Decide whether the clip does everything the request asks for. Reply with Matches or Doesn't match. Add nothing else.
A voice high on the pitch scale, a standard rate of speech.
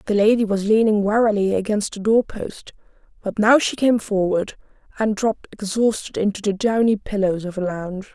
Matches